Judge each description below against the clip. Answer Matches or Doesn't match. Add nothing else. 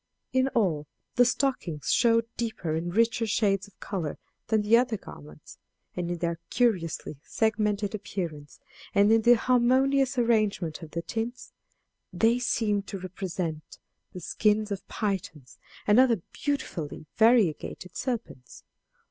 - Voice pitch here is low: Doesn't match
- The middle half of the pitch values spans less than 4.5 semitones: Doesn't match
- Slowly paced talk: Matches